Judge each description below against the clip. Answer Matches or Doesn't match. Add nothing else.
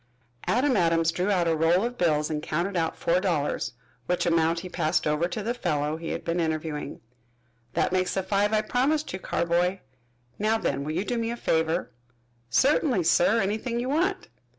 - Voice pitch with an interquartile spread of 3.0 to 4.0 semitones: Doesn't match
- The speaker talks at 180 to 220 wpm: Matches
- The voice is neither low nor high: Matches